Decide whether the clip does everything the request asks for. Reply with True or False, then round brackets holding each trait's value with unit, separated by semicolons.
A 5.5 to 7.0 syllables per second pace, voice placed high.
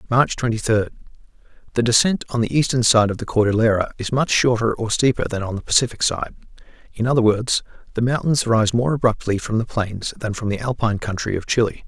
False (5.9 syllables/s; 115 Hz)